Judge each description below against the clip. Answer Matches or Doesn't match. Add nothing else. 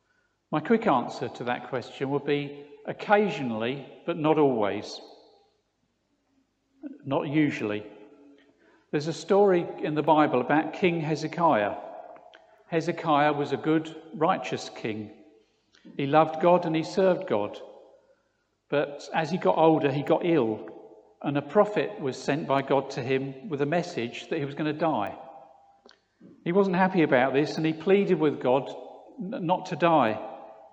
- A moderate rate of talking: Matches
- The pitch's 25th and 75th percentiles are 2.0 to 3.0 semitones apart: Doesn't match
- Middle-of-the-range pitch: Matches